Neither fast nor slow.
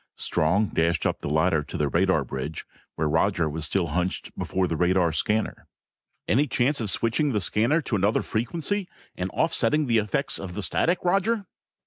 Yes: average, 175 wpm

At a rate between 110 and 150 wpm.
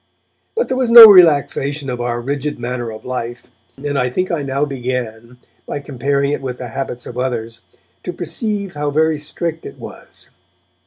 No: average, 175 wpm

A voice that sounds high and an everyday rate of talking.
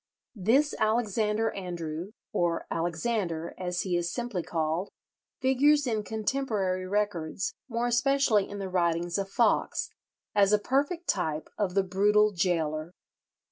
No: high, 200 Hz; slow, 130 wpm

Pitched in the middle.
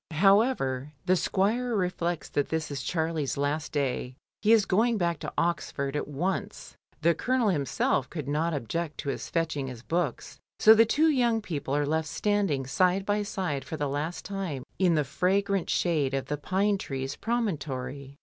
Yes: medium, 165 Hz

